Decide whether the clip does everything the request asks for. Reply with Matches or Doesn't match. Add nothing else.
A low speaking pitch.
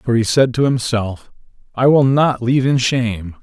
Matches